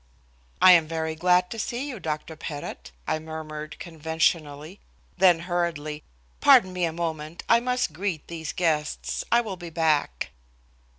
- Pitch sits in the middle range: Yes, medium, 165 Hz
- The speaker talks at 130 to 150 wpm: Yes, average, 145 wpm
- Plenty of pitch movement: No, average, 2.7 semitones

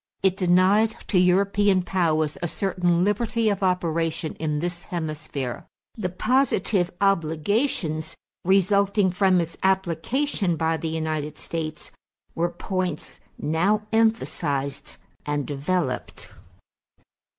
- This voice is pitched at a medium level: Yes, medium, 180 Hz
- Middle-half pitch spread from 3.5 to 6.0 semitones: Yes, average, 3.8 semitones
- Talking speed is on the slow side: Yes, slow, 105 wpm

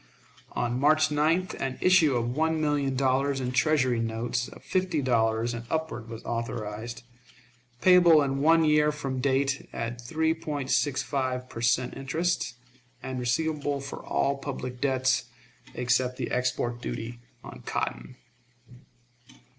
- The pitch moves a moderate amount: Yes, average, 3.9 semitones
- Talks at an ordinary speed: No, slow, 130 wpm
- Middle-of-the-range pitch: No, low, 130 Hz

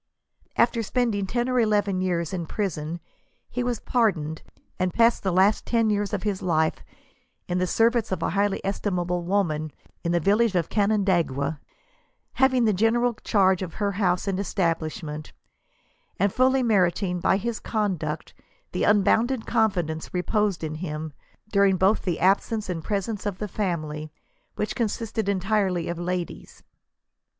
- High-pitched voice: Yes, high, 195 Hz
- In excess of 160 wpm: No, average, 155 wpm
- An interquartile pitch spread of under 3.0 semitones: No, average, 3.8 semitones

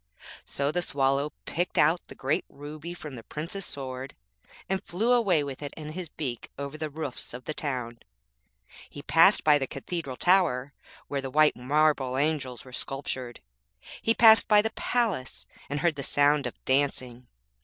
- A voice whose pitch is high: No, medium, 145 Hz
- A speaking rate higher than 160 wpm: Yes, average, 170 wpm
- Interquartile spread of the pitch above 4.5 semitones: No, average, 3.7 semitones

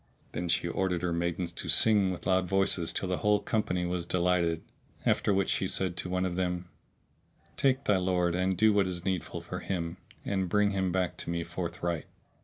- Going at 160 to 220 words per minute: Yes, average, 200 wpm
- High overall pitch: No, very low, 90 Hz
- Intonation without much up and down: Yes, narrow, 1.7 semitones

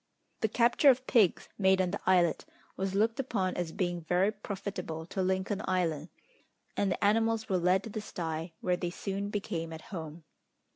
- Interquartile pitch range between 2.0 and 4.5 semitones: Yes, average, 2.9 semitones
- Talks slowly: No, average, 180 wpm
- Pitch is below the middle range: No, high, 190 Hz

